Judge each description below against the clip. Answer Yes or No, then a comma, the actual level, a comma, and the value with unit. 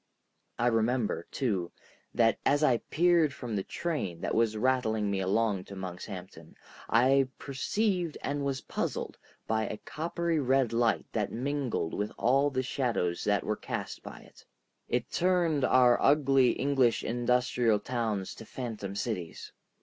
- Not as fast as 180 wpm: Yes, average, 145 wpm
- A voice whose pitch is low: Yes, low, 120 Hz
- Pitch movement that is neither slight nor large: Yes, average, 4.5 semitones